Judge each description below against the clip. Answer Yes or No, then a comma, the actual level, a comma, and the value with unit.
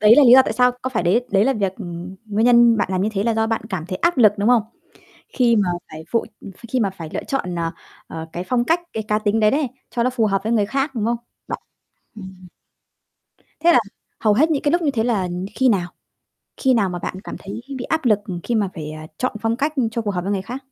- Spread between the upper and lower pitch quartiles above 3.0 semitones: Yes, average, 4.5 semitones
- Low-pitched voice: No, high, 220 Hz